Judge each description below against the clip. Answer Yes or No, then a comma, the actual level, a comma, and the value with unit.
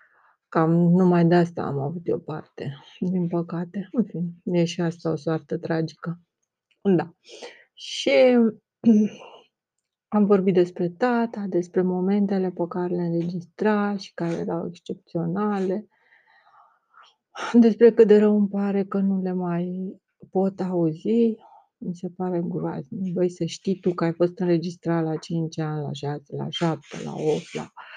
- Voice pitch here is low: No, medium, 180 Hz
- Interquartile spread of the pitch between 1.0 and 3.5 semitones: Yes, average, 3.2 semitones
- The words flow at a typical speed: Yes, average, 140 wpm